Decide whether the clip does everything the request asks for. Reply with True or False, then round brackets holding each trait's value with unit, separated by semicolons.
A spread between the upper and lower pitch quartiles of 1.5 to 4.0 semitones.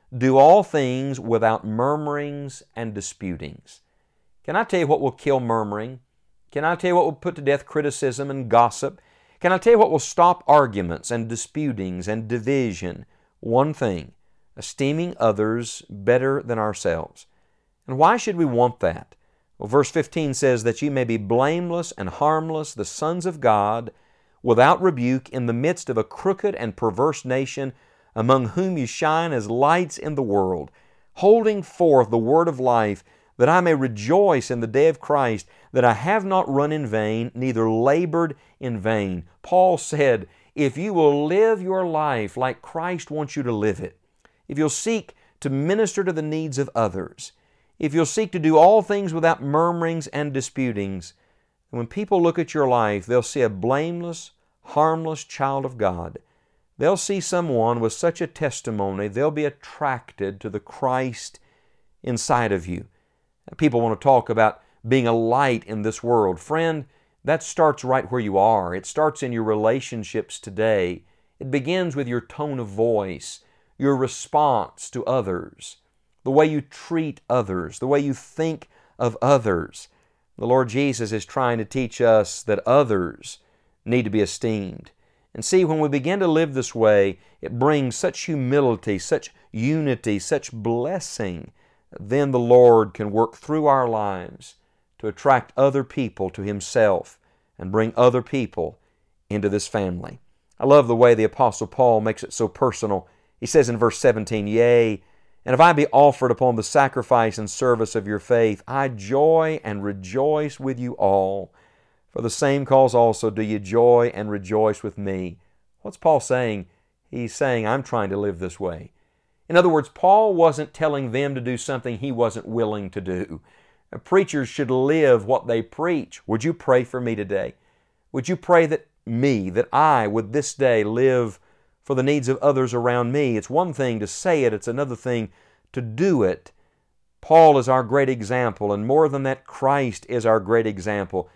False (5.3 semitones)